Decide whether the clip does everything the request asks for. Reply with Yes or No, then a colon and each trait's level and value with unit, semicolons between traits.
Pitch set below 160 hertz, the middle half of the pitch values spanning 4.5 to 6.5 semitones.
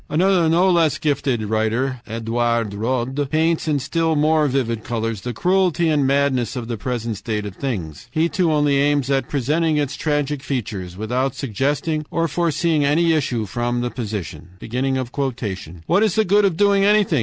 Yes: medium, 140 Hz; wide, 5.5 semitones